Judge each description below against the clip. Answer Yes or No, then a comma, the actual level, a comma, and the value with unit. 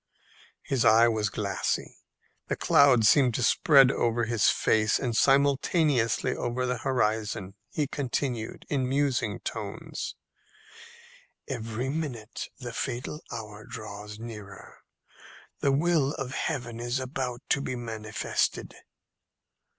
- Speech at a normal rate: No, slow, 115 wpm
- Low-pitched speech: Yes, low, 120 Hz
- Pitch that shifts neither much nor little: Yes, average, 3.6 semitones